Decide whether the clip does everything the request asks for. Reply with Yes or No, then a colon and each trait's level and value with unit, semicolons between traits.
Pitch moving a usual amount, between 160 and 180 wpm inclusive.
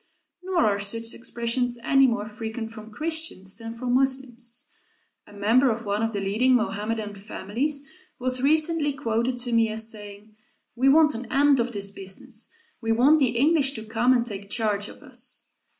Yes: average, 3.4 semitones; average, 175 wpm